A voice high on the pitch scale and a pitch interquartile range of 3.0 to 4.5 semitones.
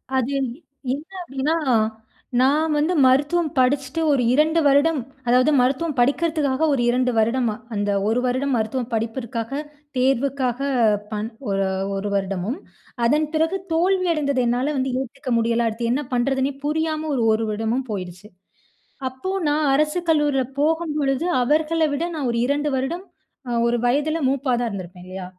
Yes: very high, 265 Hz; average, 4.2 semitones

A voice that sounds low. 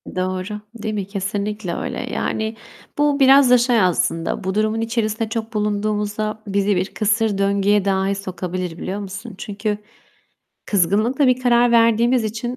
No: high, 210 Hz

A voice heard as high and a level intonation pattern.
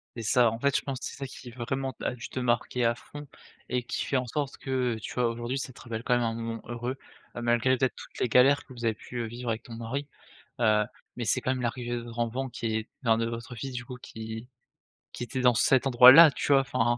No: low, 120 Hz; narrow, 1.8 semitones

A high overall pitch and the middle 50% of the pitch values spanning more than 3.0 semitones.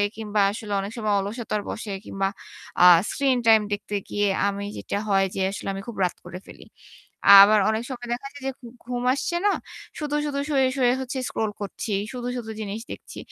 Yes: high, 220 Hz; average, 3.6 semitones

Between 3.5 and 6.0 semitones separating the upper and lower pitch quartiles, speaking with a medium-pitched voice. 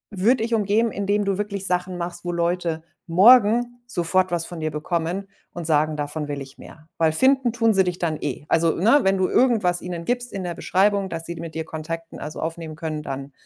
Yes: average, 3.9 semitones; medium, 175 Hz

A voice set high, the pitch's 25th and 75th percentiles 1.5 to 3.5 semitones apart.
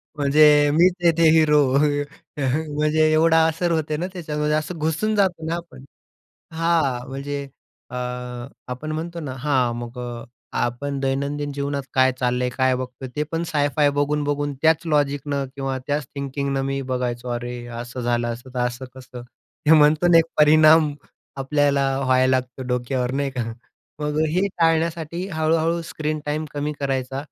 No: medium, 145 Hz; average, 3.1 semitones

